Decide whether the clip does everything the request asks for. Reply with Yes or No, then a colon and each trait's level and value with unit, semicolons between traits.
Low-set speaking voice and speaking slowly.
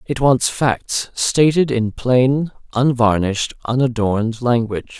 Yes: low, 120 Hz; slow, 110 wpm